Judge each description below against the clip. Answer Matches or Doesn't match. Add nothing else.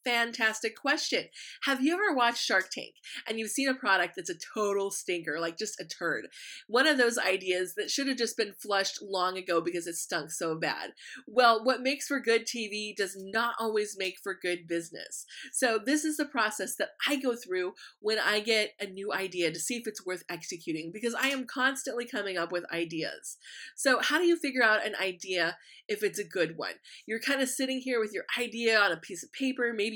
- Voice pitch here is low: Doesn't match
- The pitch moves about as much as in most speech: Doesn't match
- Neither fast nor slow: Doesn't match